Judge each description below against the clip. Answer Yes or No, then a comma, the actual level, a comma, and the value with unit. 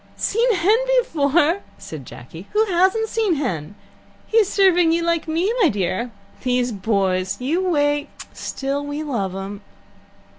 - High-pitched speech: Yes, very high, 290 Hz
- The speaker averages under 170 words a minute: Yes, average, 140 wpm